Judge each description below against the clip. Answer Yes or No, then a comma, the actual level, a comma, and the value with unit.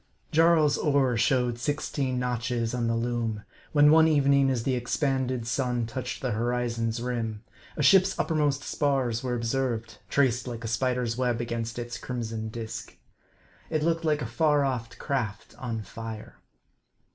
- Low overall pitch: Yes, low, 125 Hz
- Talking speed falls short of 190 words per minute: Yes, average, 150 wpm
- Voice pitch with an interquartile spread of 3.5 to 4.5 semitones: No, average, 3.1 semitones